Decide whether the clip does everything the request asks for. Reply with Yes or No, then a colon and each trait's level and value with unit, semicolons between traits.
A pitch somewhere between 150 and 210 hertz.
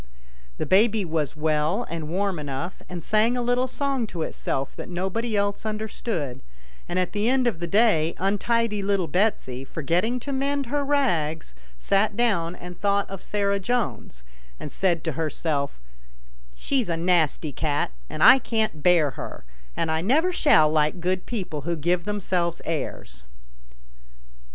Yes: medium, 185 Hz